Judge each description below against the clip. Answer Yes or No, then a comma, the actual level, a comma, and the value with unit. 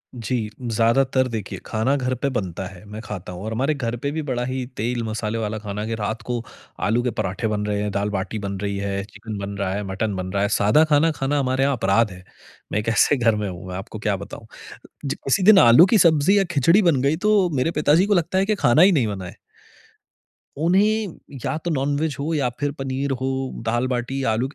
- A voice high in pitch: No, low, 120 Hz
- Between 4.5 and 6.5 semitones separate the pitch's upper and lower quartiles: Yes, wide, 5.4 semitones